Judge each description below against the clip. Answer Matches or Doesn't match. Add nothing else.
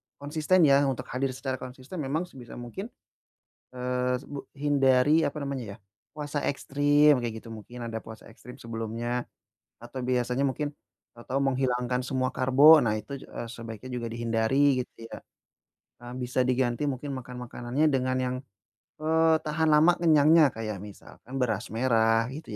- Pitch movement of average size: Matches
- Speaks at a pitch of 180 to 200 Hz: Doesn't match